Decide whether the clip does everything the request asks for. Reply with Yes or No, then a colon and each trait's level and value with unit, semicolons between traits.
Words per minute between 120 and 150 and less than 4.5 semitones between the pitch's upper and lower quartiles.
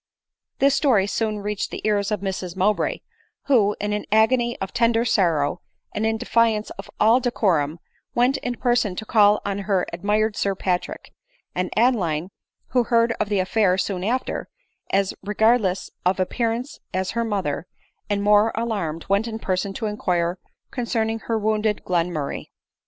No: average, 165 wpm; average, 3.3 semitones